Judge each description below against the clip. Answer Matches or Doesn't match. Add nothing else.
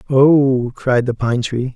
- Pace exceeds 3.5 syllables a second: Doesn't match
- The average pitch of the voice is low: Matches